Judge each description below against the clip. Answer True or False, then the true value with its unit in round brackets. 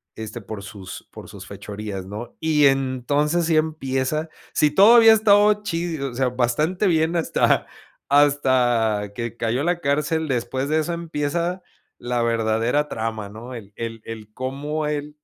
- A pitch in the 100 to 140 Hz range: True (135 Hz)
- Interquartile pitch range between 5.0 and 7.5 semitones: True (5.5 semitones)